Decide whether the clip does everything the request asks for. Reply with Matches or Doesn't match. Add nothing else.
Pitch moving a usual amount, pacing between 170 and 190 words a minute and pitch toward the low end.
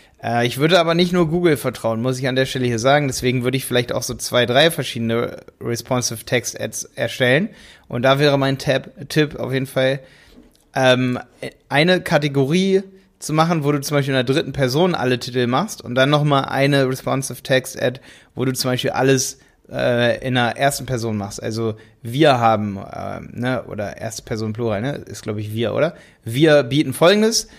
Matches